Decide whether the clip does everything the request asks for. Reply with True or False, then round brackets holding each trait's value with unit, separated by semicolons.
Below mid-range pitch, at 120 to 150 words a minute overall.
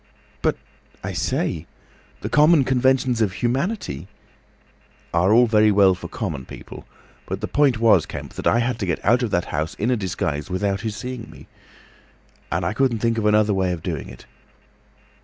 False (110 Hz; 175 wpm)